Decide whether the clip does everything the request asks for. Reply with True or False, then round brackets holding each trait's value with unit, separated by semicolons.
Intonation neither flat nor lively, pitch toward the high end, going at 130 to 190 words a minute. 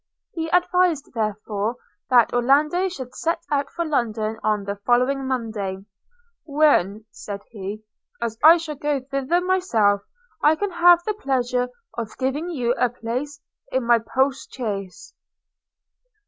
False (5.7 semitones; 260 Hz; 140 wpm)